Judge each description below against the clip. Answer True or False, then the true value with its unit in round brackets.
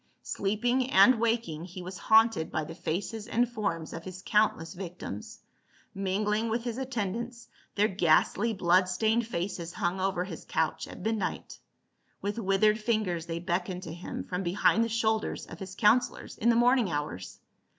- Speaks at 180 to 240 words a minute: False (160 wpm)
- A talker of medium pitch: False (195 Hz)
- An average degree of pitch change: True (4.2 semitones)